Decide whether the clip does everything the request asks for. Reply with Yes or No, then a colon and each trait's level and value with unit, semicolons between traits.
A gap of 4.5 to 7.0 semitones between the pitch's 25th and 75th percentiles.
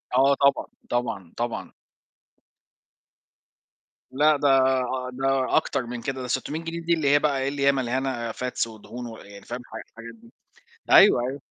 No: average, 2.8 semitones